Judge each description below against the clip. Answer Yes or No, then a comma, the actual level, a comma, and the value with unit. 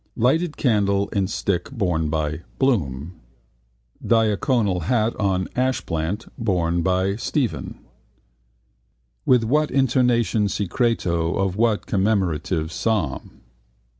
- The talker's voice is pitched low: Yes, low, 100 Hz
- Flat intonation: No, average, 5.2 semitones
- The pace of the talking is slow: Yes, slow, 95 wpm